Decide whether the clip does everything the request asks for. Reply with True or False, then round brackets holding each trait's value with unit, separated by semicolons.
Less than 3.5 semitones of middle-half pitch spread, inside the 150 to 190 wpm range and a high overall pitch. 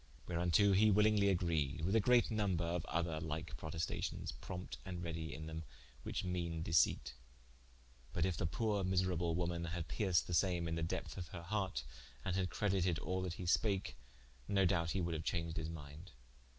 False (2.6 semitones; 185 wpm; 85 Hz)